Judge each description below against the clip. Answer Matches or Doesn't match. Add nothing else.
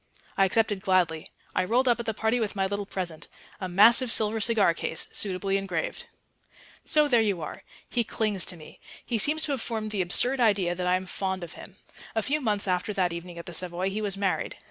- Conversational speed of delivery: Doesn't match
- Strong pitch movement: Doesn't match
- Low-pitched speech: Doesn't match